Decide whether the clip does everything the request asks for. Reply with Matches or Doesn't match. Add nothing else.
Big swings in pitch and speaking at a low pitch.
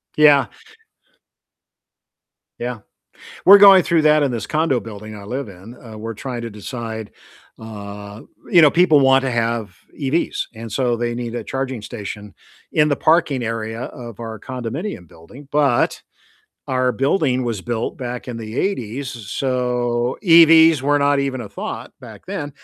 Doesn't match